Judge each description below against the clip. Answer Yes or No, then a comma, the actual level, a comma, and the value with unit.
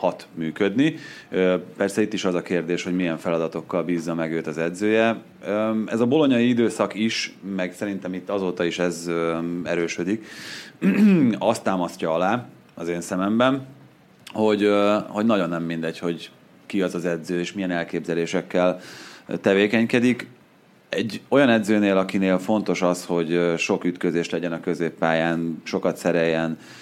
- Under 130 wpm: No, average, 140 wpm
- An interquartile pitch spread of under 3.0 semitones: No, average, 3.4 semitones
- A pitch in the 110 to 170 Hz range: No, very low, 90 Hz